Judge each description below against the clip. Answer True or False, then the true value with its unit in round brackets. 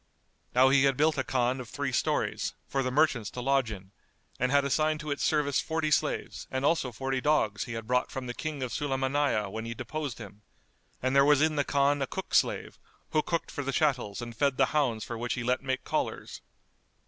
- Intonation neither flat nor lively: True (3.0 semitones)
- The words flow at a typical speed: False (225 wpm)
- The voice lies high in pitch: False (135 Hz)